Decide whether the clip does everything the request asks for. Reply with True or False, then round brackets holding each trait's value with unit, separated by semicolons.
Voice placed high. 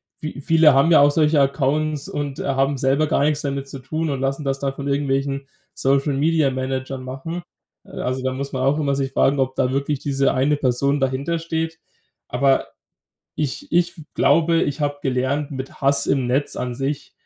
False (140 Hz)